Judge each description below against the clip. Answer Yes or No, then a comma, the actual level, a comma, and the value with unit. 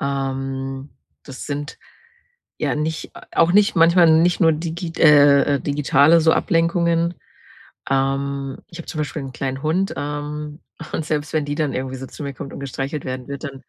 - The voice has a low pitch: No, medium, 145 Hz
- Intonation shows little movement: No, average, 3.0 semitones